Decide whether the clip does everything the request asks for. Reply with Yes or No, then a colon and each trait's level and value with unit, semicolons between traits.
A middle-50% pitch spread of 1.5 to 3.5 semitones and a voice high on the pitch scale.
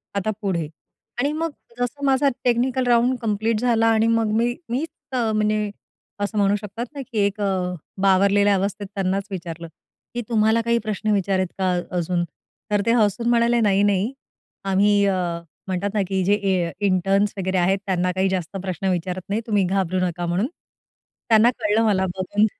Yes: average, 3.2 semitones; high, 205 Hz